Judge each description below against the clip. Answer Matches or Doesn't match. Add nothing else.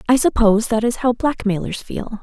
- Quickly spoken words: Doesn't match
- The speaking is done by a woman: Matches